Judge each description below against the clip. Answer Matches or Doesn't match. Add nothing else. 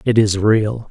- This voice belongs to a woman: Doesn't match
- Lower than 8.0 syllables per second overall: Matches